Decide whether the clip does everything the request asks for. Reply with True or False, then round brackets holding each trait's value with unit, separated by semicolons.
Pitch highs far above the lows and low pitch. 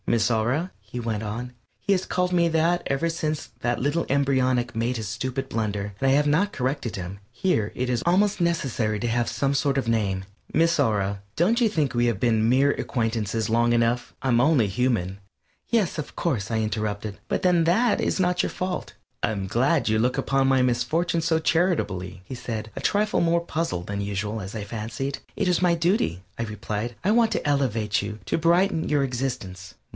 True (7.0 semitones; 125 Hz)